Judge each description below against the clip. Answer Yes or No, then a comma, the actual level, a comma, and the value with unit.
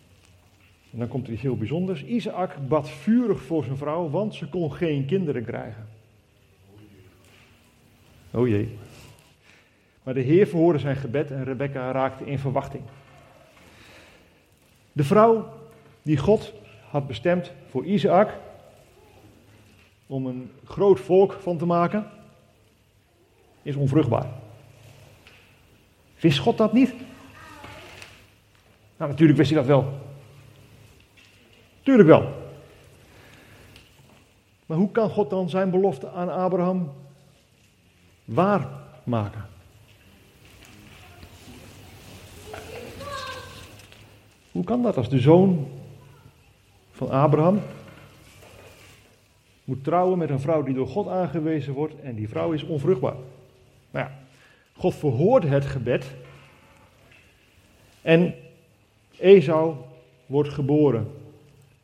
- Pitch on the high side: No, low, 130 Hz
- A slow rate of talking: Yes, slow, 100 wpm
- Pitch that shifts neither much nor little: No, wide, 6.8 semitones